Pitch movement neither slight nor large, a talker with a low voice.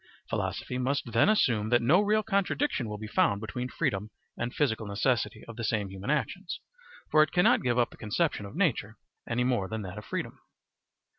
No: wide, 5.7 semitones; low, 120 Hz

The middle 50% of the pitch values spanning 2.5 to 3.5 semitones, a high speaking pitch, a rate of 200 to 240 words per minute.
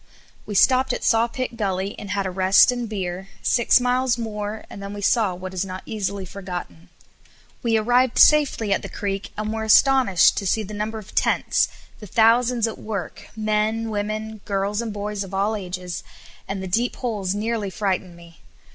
No: average, 2.8 semitones; high, 210 Hz; average, 180 wpm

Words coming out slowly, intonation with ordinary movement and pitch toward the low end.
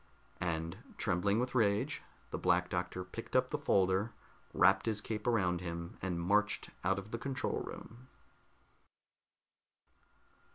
Yes: slow, 130 wpm; average, 3.4 semitones; low, 100 Hz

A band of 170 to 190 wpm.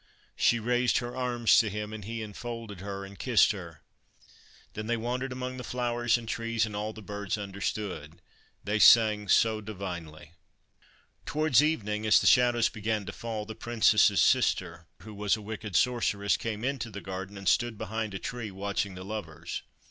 Yes: average, 175 wpm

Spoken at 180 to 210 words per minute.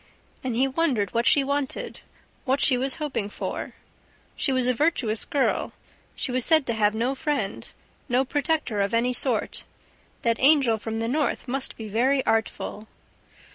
No: average, 165 wpm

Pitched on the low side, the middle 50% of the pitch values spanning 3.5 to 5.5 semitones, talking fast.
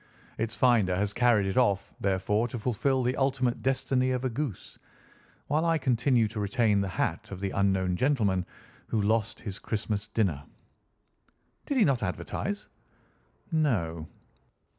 No: low, 115 Hz; average, 4.6 semitones; average, 145 wpm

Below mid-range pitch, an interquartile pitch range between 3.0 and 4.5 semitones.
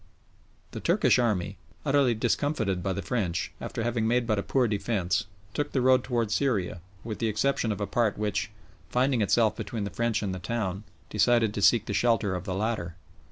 Yes: low, 110 Hz; average, 3.4 semitones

